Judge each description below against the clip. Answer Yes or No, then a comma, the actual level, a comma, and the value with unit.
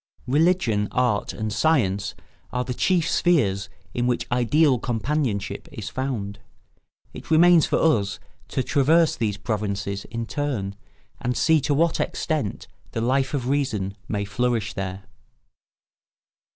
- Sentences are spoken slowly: Yes, slow, 130 wpm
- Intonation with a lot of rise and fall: Yes, wide, 6.0 semitones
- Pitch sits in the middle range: No, low, 120 Hz